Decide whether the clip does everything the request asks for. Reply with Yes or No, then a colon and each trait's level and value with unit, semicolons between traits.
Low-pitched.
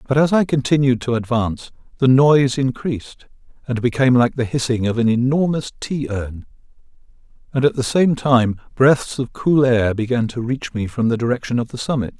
Yes: low, 125 Hz